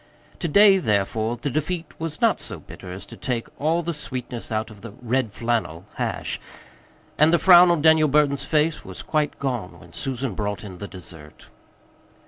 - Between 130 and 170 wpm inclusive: No, average, 180 wpm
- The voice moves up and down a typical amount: No, wide, 6.4 semitones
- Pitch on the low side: Yes, low, 130 Hz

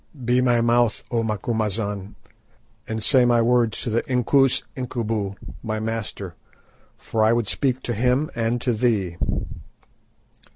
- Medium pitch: No, low, 115 Hz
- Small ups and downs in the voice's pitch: Yes, narrow, 2.2 semitones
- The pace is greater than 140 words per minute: No, slow, 135 wpm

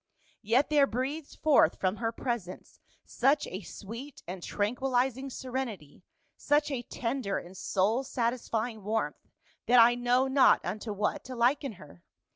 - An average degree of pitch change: Yes, average, 4.0 semitones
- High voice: Yes, high, 240 Hz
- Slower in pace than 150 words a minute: Yes, average, 140 wpm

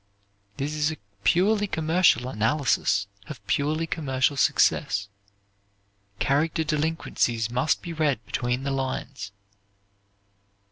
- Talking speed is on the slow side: Yes, slow, 100 wpm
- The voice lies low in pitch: No, medium, 145 Hz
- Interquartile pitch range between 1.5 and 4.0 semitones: No, average, 4.4 semitones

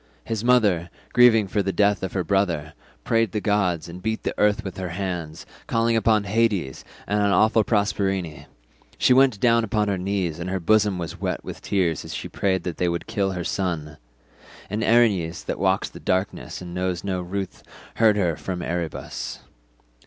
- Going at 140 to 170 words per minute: No, average, 180 wpm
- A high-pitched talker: No, very low, 95 Hz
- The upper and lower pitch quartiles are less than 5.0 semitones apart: Yes, average, 3.3 semitones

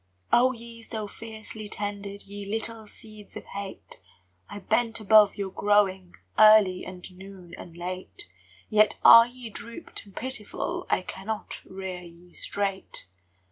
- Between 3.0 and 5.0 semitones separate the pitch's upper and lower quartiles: No, narrow, 2.6 semitones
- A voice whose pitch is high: Yes, high, 205 Hz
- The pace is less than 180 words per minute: Yes, average, 140 wpm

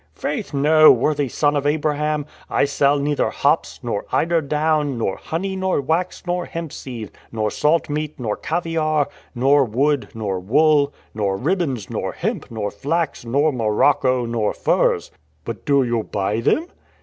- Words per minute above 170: No, average, 155 wpm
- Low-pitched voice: No, medium, 145 Hz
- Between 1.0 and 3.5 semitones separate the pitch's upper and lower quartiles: No, average, 4.9 semitones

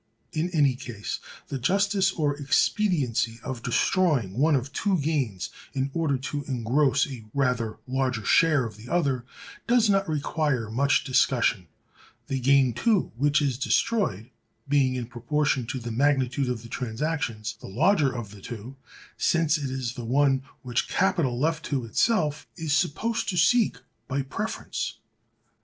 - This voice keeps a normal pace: Yes, average, 150 wpm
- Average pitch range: Yes, average, 4.3 semitones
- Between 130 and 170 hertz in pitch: Yes, low, 135 Hz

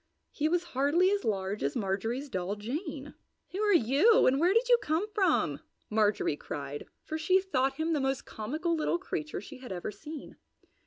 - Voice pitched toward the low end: No, very high, 290 Hz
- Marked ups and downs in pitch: Yes, wide, 8.2 semitones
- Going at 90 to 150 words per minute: No, average, 180 wpm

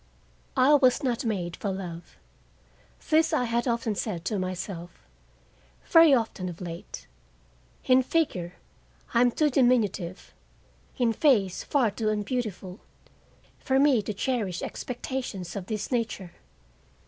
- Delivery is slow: Yes, slow, 125 wpm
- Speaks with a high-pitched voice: Yes, high, 225 Hz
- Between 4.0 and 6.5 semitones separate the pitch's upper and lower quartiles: Yes, wide, 5.5 semitones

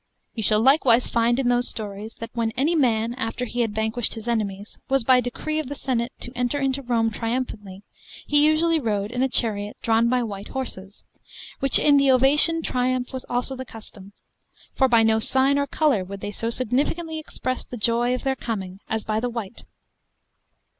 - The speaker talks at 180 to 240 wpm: Yes, average, 195 wpm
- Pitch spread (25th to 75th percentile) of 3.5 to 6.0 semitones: No, average, 3.1 semitones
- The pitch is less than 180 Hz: No, high, 240 Hz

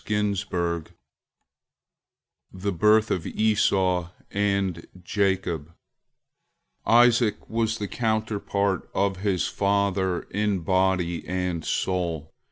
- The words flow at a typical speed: No, slow, 90 wpm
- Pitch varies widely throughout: No, narrow, 2.6 semitones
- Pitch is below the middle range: Yes, very low, 95 Hz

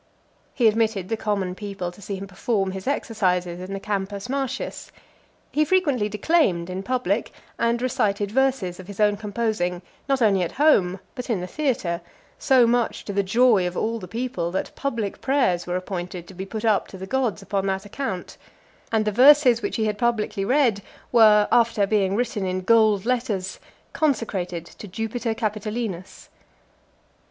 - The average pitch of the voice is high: Yes, high, 210 Hz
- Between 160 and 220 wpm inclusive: Yes, average, 170 wpm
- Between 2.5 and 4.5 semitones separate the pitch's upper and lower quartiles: Yes, average, 3.8 semitones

